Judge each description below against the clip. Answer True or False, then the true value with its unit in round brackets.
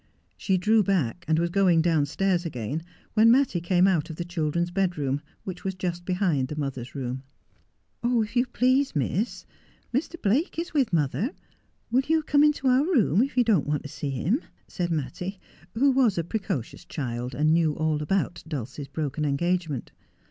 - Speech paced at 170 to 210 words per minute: True (180 wpm)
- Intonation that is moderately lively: False (6.7 semitones)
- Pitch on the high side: False (175 Hz)